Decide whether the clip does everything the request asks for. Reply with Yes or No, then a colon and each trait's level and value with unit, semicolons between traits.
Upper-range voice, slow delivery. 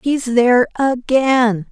Yes: high, 245 Hz; slow, 105 wpm